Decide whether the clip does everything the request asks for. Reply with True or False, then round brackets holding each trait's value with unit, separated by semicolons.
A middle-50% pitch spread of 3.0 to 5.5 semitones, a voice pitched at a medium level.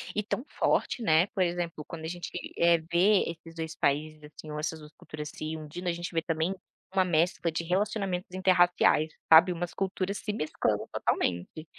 False (2.6 semitones; 170 Hz)